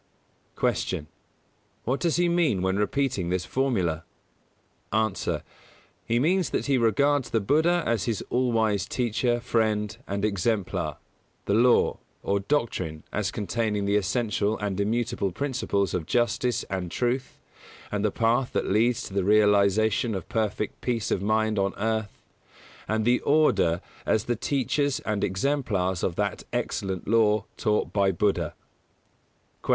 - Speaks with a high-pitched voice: No, low, 110 Hz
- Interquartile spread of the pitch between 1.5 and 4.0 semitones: Yes, average, 3.5 semitones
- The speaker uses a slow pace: No, average, 145 wpm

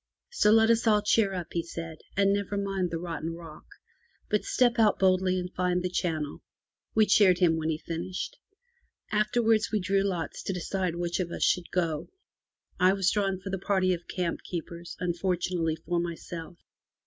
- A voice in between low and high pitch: Yes, medium, 180 Hz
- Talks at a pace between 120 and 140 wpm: No, average, 180 wpm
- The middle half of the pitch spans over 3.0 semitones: No, average, 2.7 semitones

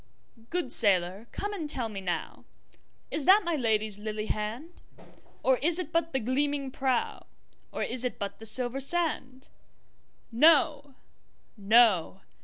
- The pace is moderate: No, slow, 120 wpm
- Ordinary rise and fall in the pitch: No, wide, 5.8 semitones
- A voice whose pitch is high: Yes, very high, 255 Hz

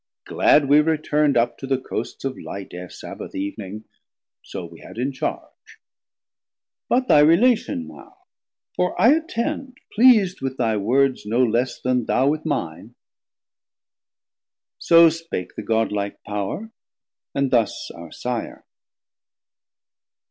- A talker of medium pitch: No, low, 130 Hz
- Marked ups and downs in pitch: Yes, wide, 7.2 semitones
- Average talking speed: No, slow, 125 wpm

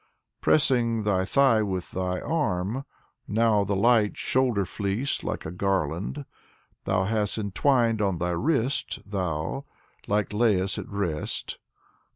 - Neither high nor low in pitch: No, low, 105 Hz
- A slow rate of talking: Yes, slow, 125 wpm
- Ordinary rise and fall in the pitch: Yes, average, 3.9 semitones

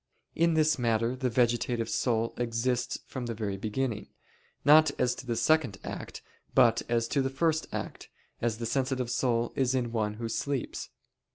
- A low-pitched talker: Yes, low, 120 Hz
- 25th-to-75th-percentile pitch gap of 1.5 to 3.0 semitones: Yes, narrow, 2.5 semitones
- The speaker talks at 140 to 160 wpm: No, average, 170 wpm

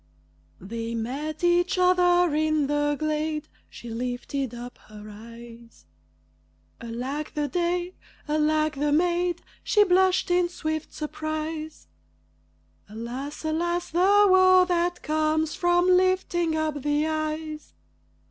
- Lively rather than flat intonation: No, average, 3.6 semitones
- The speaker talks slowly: Yes, slow, 110 wpm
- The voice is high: Yes, very high, 310 Hz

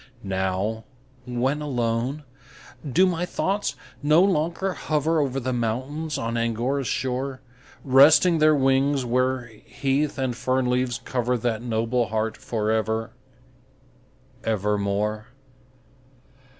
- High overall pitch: No, low, 125 Hz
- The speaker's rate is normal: No, slow, 110 wpm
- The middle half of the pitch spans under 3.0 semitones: No, average, 4.2 semitones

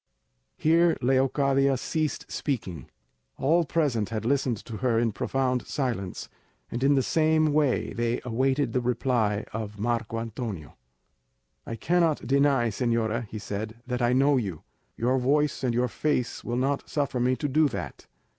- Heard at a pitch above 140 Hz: No, low, 125 Hz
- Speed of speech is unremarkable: Yes, average, 155 wpm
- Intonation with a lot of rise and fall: No, average, 3.4 semitones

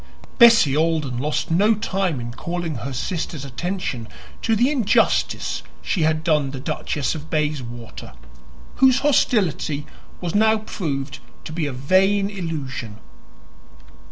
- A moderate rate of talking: No, slow, 130 wpm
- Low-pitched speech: No, medium, 160 Hz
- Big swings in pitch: Yes, wide, 6.2 semitones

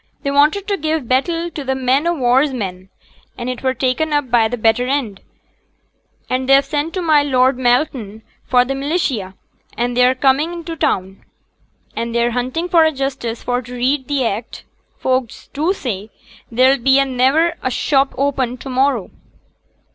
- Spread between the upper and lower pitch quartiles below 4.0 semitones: Yes, average, 3.0 semitones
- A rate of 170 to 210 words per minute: Yes, average, 175 wpm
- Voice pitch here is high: Yes, very high, 260 Hz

